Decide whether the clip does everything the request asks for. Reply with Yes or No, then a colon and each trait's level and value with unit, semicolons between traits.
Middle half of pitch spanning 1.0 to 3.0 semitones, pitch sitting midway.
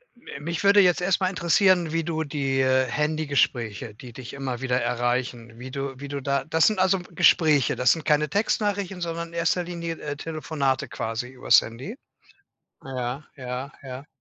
No: average, 4.7 semitones; medium, 145 Hz